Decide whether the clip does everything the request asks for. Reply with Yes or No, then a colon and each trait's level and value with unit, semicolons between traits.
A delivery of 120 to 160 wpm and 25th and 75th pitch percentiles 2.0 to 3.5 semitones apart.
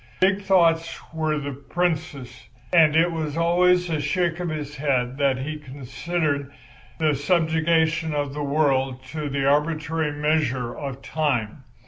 Yes: average, 145 wpm; average, 2.8 semitones